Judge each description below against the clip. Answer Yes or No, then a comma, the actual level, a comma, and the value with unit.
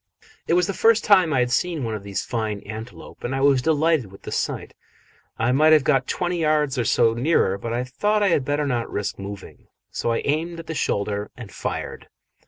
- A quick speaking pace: Yes, fast, 220 wpm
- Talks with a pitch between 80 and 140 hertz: Yes, low, 135 Hz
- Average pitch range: No, wide, 6.2 semitones